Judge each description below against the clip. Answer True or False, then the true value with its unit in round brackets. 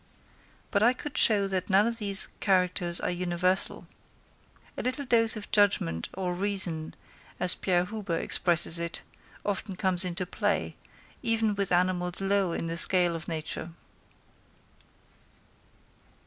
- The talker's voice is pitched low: False (185 Hz)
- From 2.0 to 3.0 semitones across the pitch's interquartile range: True (2.7 semitones)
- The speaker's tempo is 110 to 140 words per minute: True (135 wpm)